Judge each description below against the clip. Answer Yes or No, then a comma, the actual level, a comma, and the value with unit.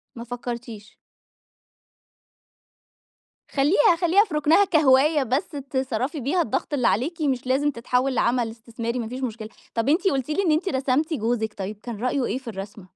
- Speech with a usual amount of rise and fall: Yes, average, 4.3 semitones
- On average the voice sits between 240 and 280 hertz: Yes, very high, 255 Hz